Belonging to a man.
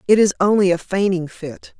No: female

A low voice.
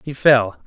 Yes: low, 125 Hz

